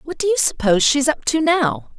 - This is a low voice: No, very high, 275 Hz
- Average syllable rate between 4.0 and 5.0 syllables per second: No, 5.3 syllables/s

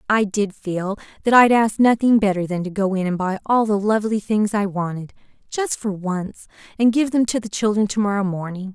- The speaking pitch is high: Yes, high, 205 Hz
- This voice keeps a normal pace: No, fast, 215 wpm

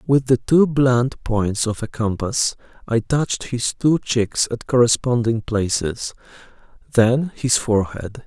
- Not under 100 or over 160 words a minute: Yes, average, 140 wpm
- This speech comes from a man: Yes, male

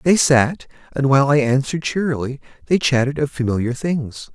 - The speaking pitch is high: No, medium, 140 Hz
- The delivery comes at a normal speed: Yes, average, 165 wpm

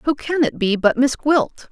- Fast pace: Yes, fast, 245 wpm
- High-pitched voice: Yes, very high, 265 Hz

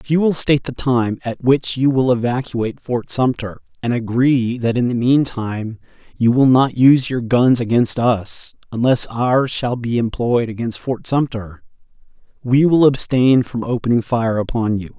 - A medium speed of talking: Yes, average, 175 wpm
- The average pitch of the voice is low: Yes, low, 125 Hz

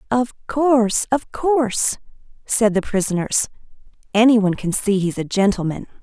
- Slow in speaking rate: Yes, slow, 120 wpm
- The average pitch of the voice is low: No, high, 220 Hz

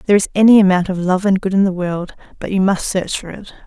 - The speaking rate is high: Yes, fast, 280 wpm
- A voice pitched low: No, high, 190 Hz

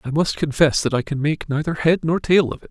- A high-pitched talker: No, medium, 150 Hz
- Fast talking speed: Yes, fast, 290 wpm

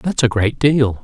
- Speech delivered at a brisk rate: Yes, fast, 230 wpm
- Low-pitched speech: Yes, low, 125 Hz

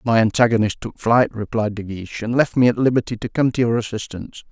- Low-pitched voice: Yes, low, 115 Hz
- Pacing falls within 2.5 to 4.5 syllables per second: No, 6.2 syllables/s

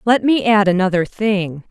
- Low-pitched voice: No, high, 200 Hz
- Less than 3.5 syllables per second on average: No, 4.5 syllables/s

